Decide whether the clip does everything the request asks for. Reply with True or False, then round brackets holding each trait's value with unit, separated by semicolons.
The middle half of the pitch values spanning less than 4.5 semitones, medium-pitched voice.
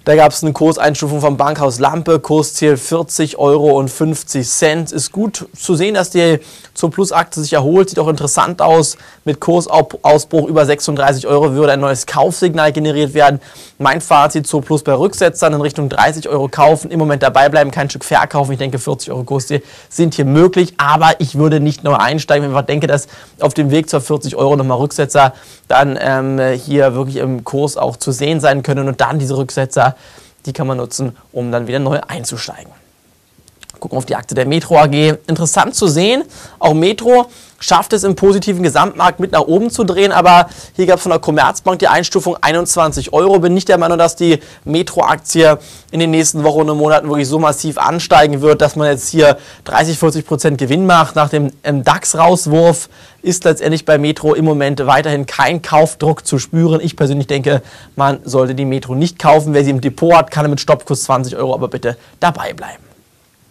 True (2.7 semitones; 150 Hz)